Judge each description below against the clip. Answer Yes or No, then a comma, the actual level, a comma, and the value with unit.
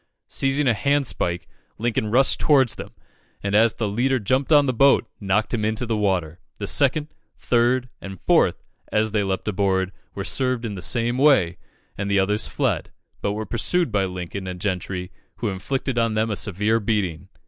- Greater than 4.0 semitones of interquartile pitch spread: Yes, average, 4.5 semitones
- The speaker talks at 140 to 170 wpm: No, average, 185 wpm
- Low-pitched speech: Yes, low, 110 Hz